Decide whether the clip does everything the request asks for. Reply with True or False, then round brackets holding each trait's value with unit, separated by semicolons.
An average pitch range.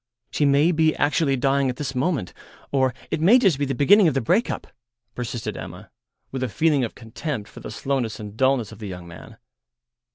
True (4.6 semitones)